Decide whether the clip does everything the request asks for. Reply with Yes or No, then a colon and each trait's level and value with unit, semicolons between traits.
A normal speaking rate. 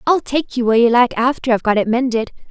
No: fast, 265 wpm